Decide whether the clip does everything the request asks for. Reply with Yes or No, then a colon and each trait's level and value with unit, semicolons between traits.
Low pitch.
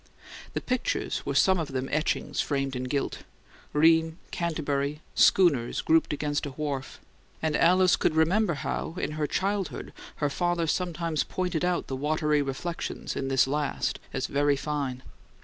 No: medium, 150 Hz